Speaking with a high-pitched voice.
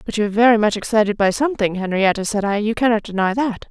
Yes: high, 215 Hz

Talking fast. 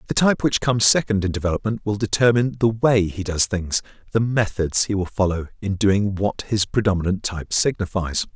No: average, 180 wpm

